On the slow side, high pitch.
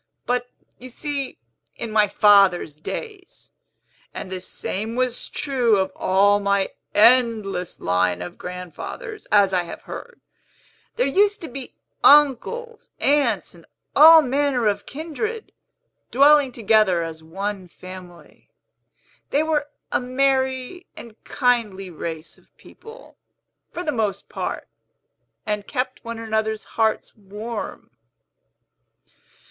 Yes: slow, 120 wpm; high, 230 Hz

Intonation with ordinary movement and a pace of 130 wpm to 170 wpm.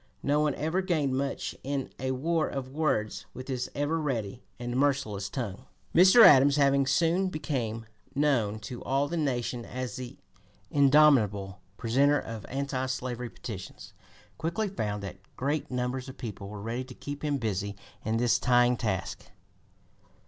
Yes: average, 3.9 semitones; average, 155 wpm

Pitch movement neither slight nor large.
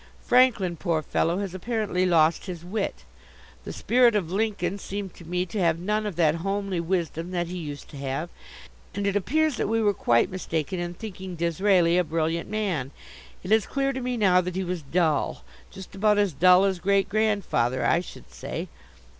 Yes: average, 3.3 semitones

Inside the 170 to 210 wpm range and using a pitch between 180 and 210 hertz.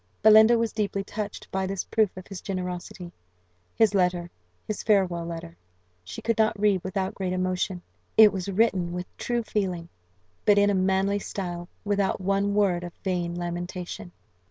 No: average, 160 wpm; high, 190 Hz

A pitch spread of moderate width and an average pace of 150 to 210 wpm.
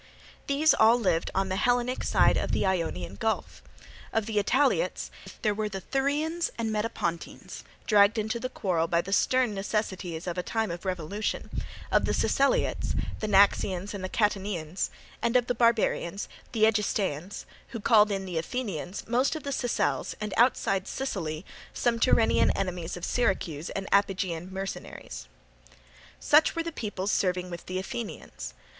Yes: average, 4.2 semitones; average, 155 wpm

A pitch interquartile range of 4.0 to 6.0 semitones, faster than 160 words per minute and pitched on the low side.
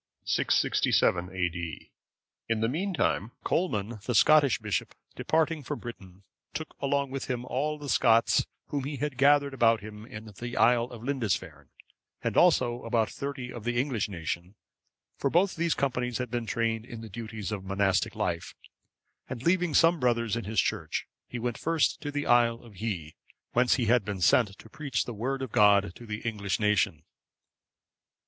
Yes: average, 4.6 semitones; average, 170 wpm; low, 120 Hz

